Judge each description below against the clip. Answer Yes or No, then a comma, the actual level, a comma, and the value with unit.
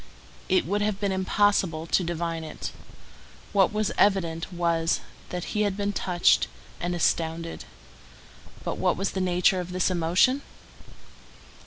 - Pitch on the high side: No, medium, 180 Hz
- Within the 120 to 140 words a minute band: Yes, slow, 135 wpm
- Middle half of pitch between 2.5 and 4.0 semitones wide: Yes, average, 2.9 semitones